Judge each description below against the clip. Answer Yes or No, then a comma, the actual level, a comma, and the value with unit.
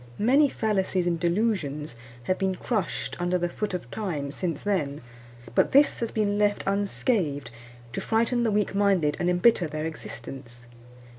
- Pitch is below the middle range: No, medium, 185 Hz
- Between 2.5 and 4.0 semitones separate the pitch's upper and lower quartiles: No, average, 5.2 semitones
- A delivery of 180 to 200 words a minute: No, average, 155 wpm